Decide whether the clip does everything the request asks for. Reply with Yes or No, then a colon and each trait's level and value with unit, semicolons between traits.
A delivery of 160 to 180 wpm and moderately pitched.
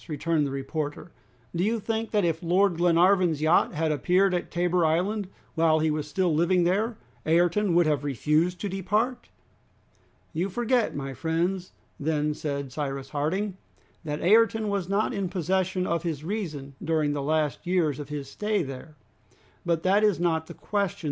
Yes: average, 170 wpm; medium, 170 Hz